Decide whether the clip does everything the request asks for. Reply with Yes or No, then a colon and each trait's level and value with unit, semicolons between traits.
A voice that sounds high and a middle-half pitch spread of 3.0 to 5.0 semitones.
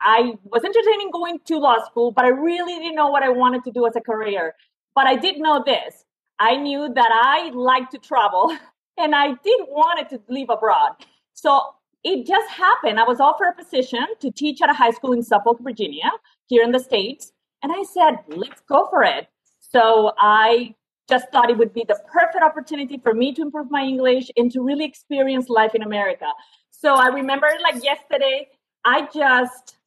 Yes: very high, 275 Hz; average, 4.5 semitones